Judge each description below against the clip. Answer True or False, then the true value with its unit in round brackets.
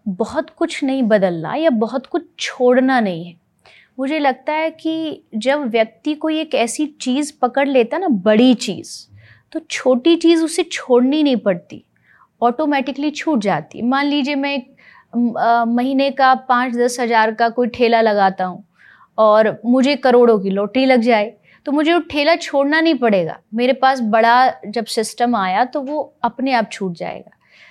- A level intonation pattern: False (4.2 semitones)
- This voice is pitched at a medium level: False (250 Hz)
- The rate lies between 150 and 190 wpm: True (160 wpm)